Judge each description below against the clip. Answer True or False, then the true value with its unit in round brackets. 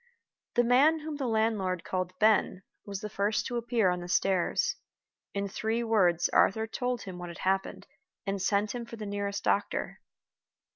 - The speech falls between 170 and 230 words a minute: True (175 wpm)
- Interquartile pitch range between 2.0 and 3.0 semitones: False (3.4 semitones)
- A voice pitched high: True (205 Hz)